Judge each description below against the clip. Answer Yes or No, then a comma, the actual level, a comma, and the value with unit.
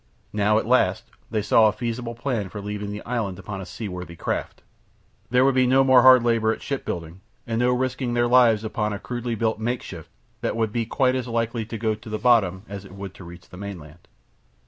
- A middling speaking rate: No, fast, 220 wpm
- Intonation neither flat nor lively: Yes, average, 3.2 semitones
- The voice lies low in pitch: Yes, low, 110 Hz